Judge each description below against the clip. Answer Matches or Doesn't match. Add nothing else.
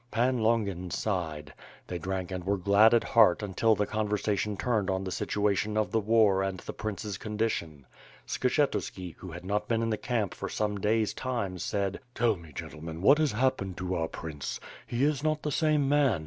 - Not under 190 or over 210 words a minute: Matches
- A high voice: Doesn't match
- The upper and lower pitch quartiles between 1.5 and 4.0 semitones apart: Matches